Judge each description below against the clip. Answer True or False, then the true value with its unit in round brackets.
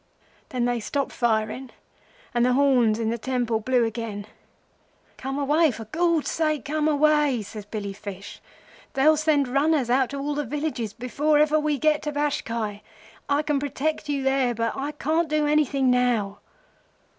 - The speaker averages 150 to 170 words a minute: True (160 wpm)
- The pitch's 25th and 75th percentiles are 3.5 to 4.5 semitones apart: True (4.2 semitones)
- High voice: True (270 Hz)